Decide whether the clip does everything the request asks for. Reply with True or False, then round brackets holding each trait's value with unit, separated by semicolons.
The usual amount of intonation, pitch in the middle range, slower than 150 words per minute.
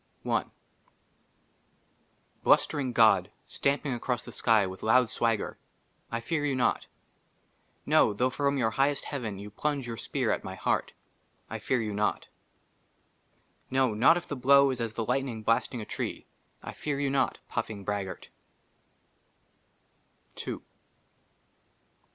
False (4.1 semitones; 120 Hz; 135 wpm)